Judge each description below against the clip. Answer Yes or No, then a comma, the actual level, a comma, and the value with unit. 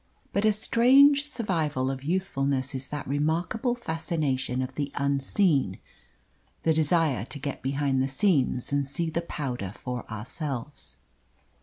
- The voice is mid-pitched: Yes, medium, 145 Hz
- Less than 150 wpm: Yes, slow, 135 wpm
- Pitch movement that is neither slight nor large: Yes, average, 4.3 semitones